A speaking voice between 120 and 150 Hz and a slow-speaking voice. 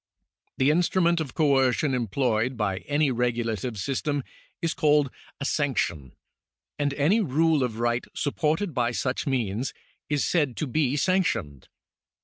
Yes: low, 135 Hz; slow, 130 wpm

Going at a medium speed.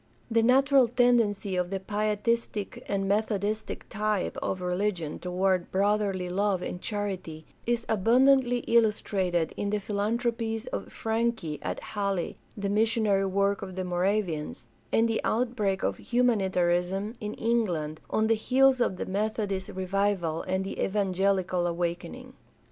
No: slow, 130 wpm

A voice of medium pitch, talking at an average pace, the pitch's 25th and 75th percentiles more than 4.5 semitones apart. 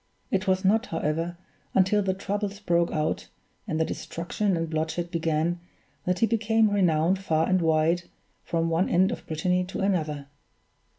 No: medium, 175 Hz; average, 160 wpm; average, 3.0 semitones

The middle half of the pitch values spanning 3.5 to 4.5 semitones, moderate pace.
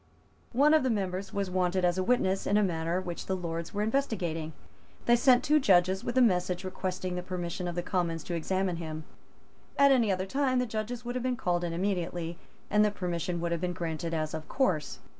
No: average, 4.1 semitones; fast, 215 wpm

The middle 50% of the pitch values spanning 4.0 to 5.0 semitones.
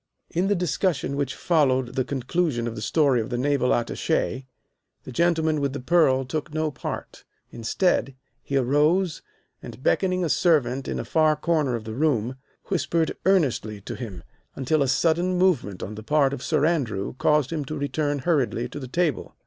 Yes: average, 4.3 semitones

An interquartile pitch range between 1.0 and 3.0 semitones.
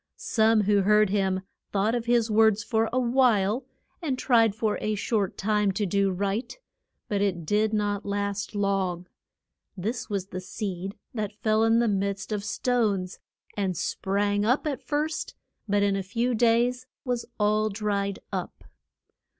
Yes: narrow, 2.5 semitones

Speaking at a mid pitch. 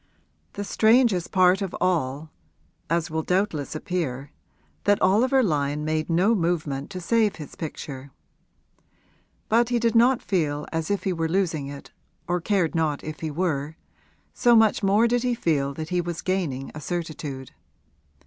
Yes: medium, 170 Hz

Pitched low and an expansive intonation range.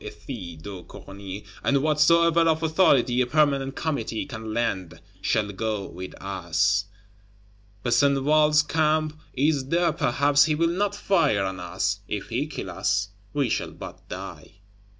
Yes: low, 130 Hz; wide, 7.2 semitones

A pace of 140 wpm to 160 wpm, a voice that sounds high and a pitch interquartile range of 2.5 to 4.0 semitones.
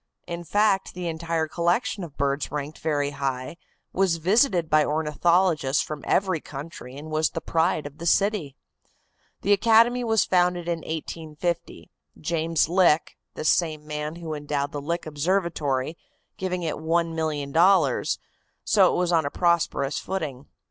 No: average, 145 wpm; medium, 165 Hz; average, 2.9 semitones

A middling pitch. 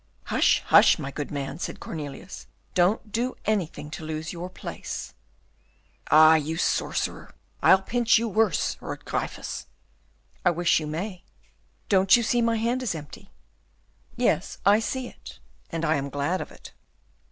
Yes: medium, 180 Hz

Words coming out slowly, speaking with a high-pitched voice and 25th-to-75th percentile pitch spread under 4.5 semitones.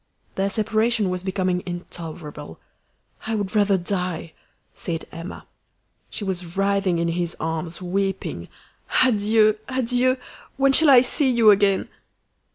Yes: slow, 125 wpm; high, 195 Hz; average, 3.8 semitones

